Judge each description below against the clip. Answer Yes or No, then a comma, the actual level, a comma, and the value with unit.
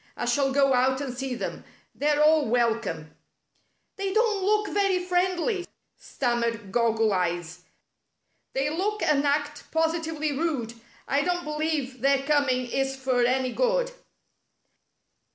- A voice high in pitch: Yes, very high, 280 Hz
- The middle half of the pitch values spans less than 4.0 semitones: No, average, 5.1 semitones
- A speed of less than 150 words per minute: Yes, slow, 135 wpm